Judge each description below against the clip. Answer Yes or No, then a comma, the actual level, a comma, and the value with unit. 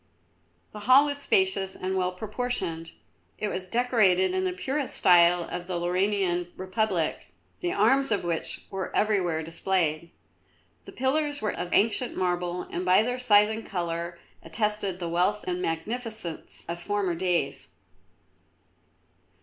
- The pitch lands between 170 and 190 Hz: Yes, medium, 185 Hz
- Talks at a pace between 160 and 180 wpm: No, average, 140 wpm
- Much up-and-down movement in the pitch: No, average, 3.8 semitones